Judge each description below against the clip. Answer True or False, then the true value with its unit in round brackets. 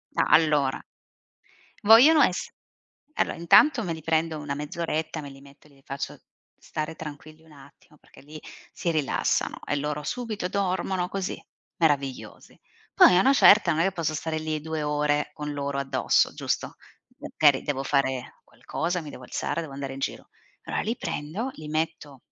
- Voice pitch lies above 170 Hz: False (155 Hz)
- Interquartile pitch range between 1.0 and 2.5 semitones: False (2.9 semitones)